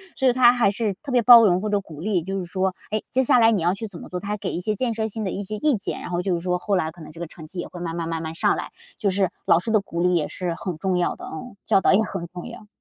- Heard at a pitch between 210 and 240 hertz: No, high, 190 Hz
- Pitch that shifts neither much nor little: Yes, average, 3.7 semitones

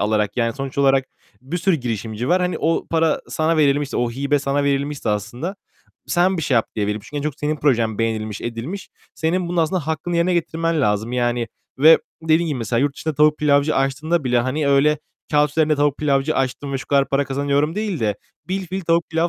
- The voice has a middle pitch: Yes, medium, 145 Hz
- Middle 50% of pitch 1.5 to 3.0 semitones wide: No, average, 4.4 semitones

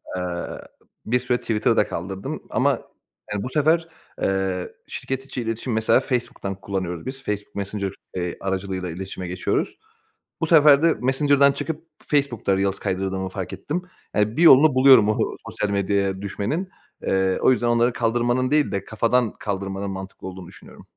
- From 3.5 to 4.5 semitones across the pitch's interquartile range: No, average, 5.3 semitones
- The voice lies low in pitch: Yes, low, 105 Hz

